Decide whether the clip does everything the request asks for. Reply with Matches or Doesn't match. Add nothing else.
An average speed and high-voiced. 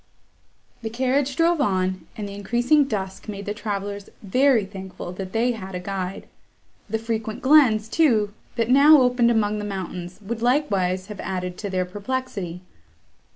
Matches